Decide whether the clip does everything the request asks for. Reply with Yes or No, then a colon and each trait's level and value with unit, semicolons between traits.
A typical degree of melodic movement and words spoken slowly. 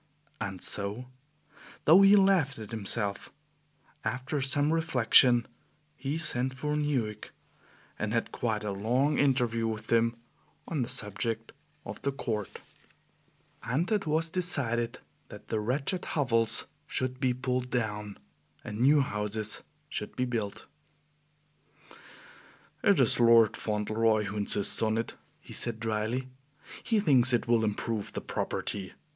Yes: average, 4.1 semitones; slow, 130 wpm